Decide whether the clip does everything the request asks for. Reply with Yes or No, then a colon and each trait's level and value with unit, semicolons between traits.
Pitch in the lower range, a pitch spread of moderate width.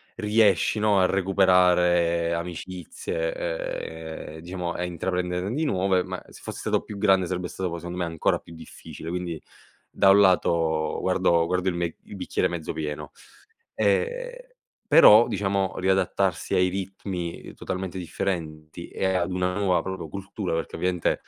No: very low, 90 Hz; narrow, 2.2 semitones